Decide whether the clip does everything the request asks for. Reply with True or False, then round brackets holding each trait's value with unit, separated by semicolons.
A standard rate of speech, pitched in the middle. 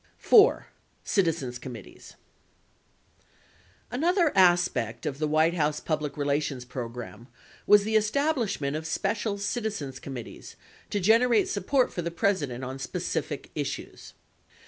False (115 wpm; 165 Hz)